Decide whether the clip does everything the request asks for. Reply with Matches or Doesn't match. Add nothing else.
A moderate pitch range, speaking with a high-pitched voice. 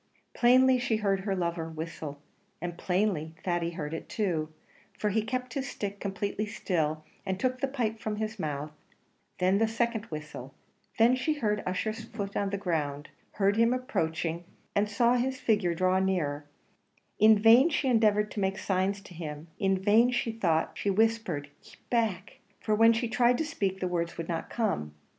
Matches